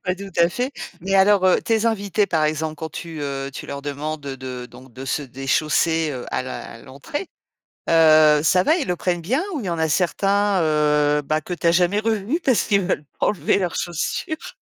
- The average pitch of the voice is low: No, medium, 165 Hz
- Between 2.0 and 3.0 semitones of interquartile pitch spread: No, average, 4.9 semitones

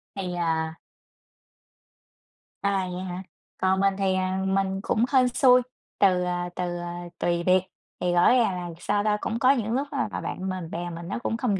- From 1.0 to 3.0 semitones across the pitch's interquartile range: Yes, average, 2.7 semitones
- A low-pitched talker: No, medium, 185 Hz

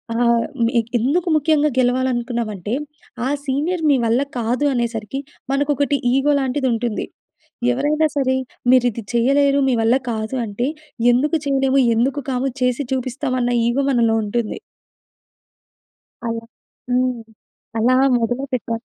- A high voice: Yes, very high, 255 Hz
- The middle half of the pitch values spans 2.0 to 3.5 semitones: Yes, average, 2.8 semitones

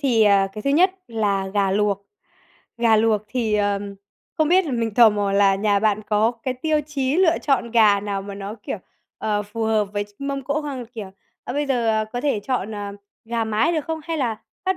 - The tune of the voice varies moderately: Yes, average, 4.8 semitones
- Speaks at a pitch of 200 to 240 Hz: Yes, high, 225 Hz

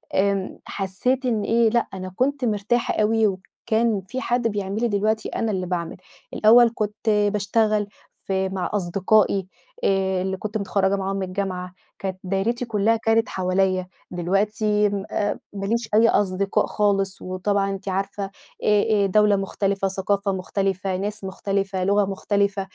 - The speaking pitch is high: Yes, high, 200 Hz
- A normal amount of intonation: No, narrow, 1.9 semitones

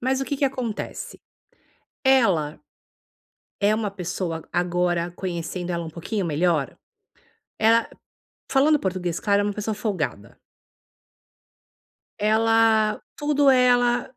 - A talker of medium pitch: No, high, 205 Hz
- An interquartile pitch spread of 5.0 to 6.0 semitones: Yes, wide, 5.5 semitones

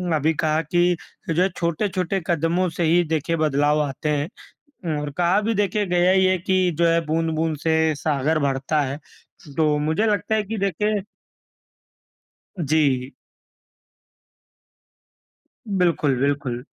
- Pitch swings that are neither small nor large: Yes, average, 3.5 semitones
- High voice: No, medium, 165 Hz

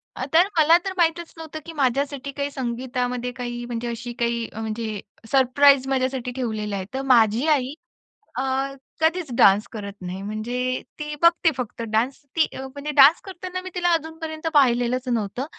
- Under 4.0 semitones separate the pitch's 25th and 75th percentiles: No, average, 4.4 semitones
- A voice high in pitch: Yes, very high, 260 Hz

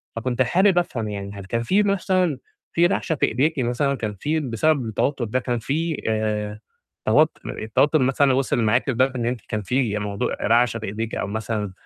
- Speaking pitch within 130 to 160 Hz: No, low, 120 Hz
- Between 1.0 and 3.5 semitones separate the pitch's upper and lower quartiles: No, average, 5.1 semitones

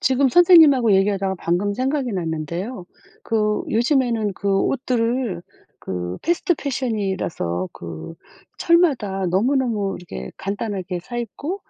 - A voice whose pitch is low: No, high, 210 Hz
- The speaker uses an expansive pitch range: Yes, wide, 6.0 semitones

